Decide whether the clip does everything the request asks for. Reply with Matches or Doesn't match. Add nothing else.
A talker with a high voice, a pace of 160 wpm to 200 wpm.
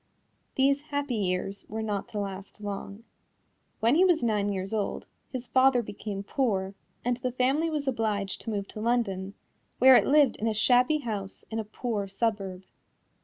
Matches